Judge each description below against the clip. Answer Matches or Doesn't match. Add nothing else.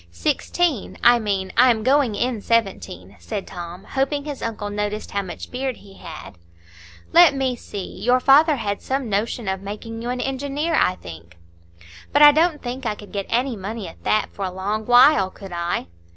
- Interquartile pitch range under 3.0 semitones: Doesn't match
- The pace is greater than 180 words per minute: Matches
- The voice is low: Doesn't match